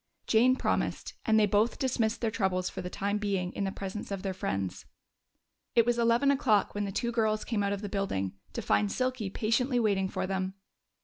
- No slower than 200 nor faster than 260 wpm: Yes, fast, 205 wpm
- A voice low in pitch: No, high, 210 Hz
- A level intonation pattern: No, average, 3.2 semitones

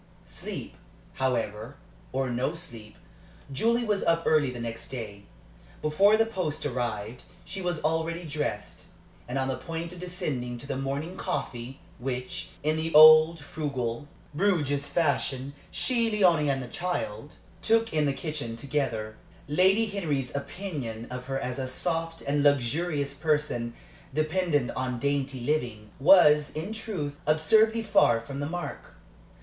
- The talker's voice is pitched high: No, medium, 145 Hz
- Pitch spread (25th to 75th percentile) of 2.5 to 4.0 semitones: No, average, 4.8 semitones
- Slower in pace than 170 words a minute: Yes, average, 145 wpm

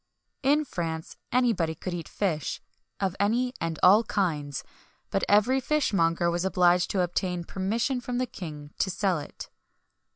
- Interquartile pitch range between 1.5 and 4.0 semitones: No, wide, 5.5 semitones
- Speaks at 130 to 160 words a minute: Yes, average, 150 wpm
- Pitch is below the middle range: No, medium, 185 Hz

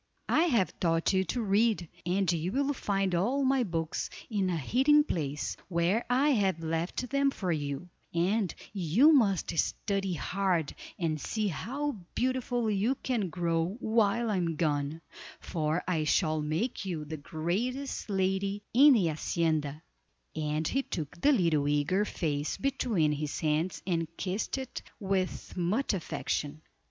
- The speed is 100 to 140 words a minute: No, average, 150 wpm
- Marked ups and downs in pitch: Yes, wide, 5.9 semitones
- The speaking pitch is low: No, medium, 185 Hz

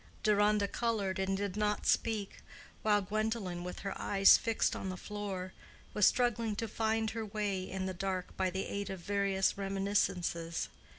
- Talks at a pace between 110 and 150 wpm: No, average, 165 wpm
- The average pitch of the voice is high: Yes, high, 200 Hz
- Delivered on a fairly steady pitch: Yes, narrow, 2.0 semitones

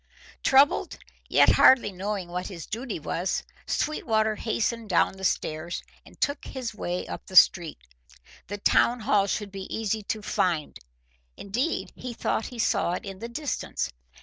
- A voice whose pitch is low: No, high, 210 Hz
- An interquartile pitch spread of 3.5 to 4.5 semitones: Yes, average, 4.0 semitones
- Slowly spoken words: No, average, 155 wpm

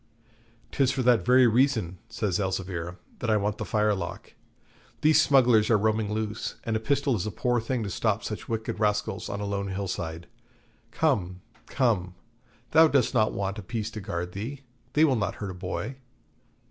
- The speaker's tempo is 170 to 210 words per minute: Yes, average, 185 wpm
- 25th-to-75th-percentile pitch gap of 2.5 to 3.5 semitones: No, average, 4.0 semitones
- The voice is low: Yes, low, 105 Hz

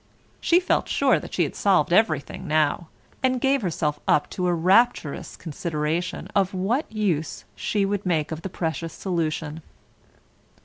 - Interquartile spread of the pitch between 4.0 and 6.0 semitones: Yes, average, 4.5 semitones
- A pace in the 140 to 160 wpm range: Yes, average, 150 wpm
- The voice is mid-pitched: Yes, medium, 175 Hz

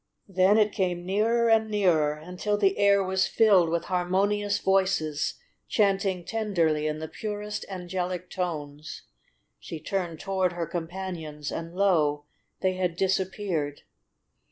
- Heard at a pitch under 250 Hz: Yes, medium, 185 Hz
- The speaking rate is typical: No, slow, 130 wpm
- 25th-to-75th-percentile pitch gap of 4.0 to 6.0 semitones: No, average, 3.2 semitones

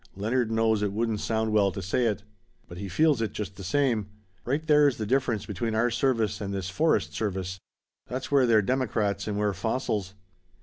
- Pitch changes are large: No, average, 3.6 semitones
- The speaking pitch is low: Yes, low, 110 Hz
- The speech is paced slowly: No, average, 190 wpm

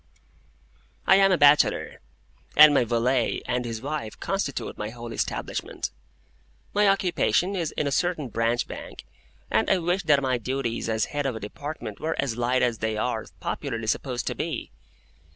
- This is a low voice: Yes, low, 130 Hz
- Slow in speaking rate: No, average, 170 wpm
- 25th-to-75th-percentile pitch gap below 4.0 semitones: No, average, 5.1 semitones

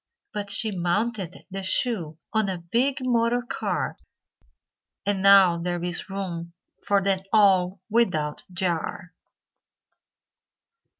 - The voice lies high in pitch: Yes, high, 195 Hz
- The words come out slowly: Yes, slow, 110 wpm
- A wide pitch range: No, average, 3.7 semitones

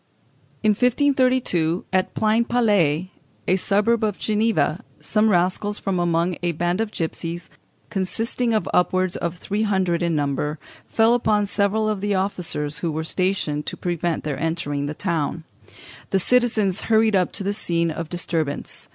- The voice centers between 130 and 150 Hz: No, medium, 185 Hz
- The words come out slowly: No, average, 150 wpm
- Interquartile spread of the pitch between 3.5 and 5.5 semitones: Yes, average, 4.4 semitones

